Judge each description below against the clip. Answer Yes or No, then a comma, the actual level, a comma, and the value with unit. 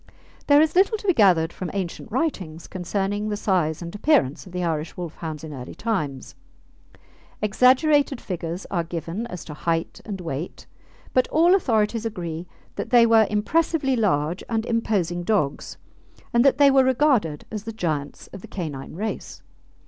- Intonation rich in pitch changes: Yes, wide, 6.2 semitones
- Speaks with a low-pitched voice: No, high, 200 Hz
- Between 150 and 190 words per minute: Yes, average, 165 wpm